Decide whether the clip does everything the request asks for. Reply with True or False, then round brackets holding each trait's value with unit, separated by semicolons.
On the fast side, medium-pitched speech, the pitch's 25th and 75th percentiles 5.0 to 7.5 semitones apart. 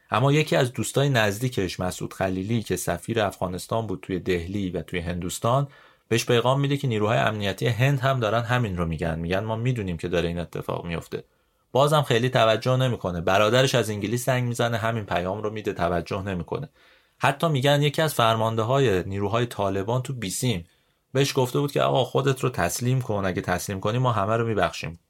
False (185 wpm; 110 Hz; 5.4 semitones)